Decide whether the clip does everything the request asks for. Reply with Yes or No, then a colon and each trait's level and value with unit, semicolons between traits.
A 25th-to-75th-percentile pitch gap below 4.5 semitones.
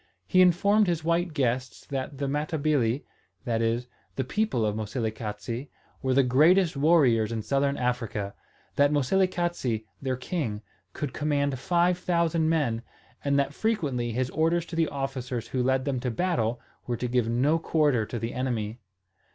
No: average, 5.1 semitones